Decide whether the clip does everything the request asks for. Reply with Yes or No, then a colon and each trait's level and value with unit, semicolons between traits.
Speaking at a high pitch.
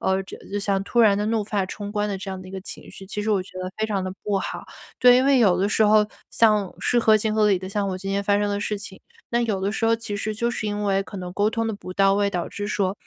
Yes: high, 205 Hz